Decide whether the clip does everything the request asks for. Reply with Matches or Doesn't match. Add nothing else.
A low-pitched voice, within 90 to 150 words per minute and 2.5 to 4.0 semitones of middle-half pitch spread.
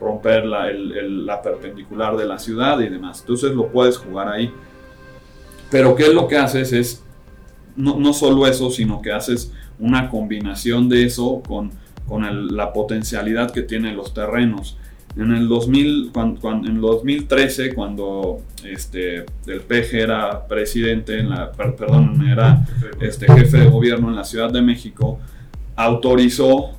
Doesn't match